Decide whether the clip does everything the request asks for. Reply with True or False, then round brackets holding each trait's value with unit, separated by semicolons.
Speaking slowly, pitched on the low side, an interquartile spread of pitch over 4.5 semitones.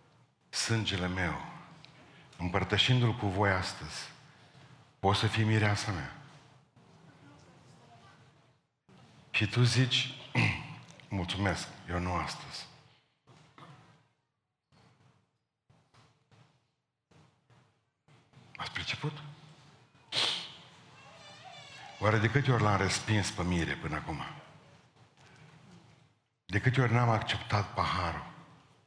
True (75 wpm; 130 Hz; 5.2 semitones)